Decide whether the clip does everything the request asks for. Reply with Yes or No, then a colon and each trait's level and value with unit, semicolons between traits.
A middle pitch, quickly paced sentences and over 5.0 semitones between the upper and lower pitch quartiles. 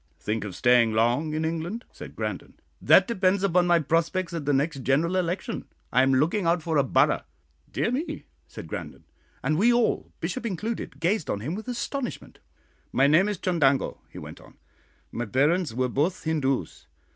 No: medium, 165 Hz; average, 180 wpm; wide, 5.5 semitones